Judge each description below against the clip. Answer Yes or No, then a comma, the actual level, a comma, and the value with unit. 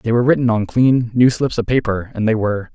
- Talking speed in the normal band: No, fast, 260 wpm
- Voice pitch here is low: Yes, low, 115 Hz